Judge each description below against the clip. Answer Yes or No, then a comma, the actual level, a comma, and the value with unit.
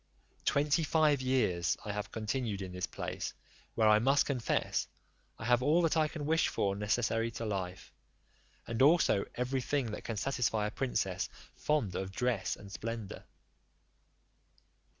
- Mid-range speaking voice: No, low, 115 Hz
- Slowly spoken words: No, average, 150 wpm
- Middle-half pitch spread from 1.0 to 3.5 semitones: No, average, 5.0 semitones